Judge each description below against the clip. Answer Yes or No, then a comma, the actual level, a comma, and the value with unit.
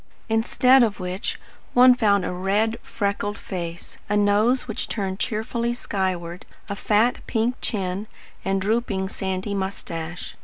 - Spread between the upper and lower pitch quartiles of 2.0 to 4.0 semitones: Yes, average, 2.9 semitones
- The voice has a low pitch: No, high, 205 Hz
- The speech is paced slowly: Yes, slow, 130 wpm